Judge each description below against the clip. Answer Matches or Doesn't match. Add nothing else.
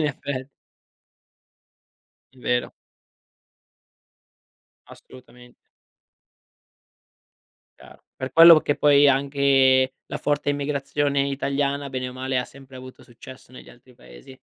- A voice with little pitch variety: Matches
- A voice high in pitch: Doesn't match